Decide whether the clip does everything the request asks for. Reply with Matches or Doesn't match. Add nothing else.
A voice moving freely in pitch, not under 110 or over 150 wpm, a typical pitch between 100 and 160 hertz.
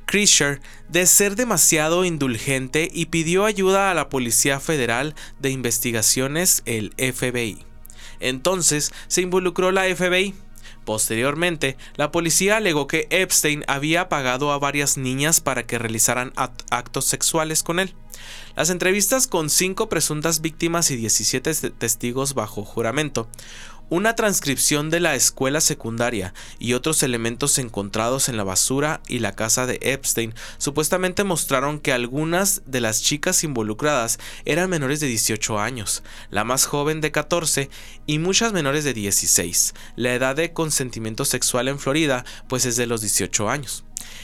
Matches